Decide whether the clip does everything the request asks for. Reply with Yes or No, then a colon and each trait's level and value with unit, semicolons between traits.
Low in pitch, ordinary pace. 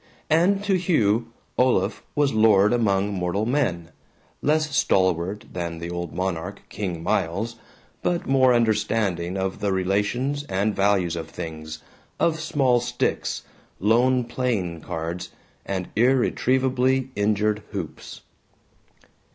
No: low, 105 Hz; slow, 115 wpm